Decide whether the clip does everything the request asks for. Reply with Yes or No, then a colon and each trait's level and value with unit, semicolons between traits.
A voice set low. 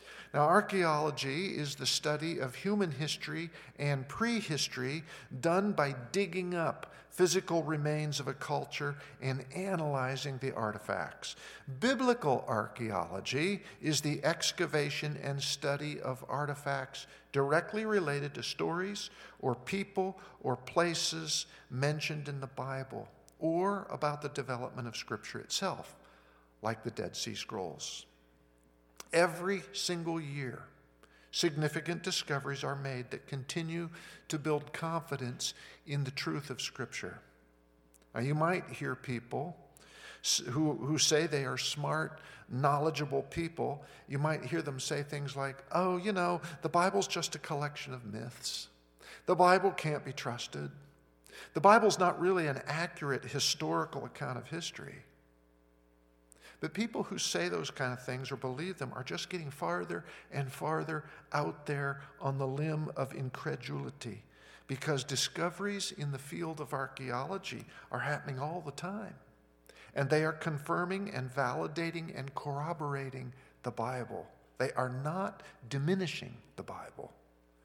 No: medium, 145 Hz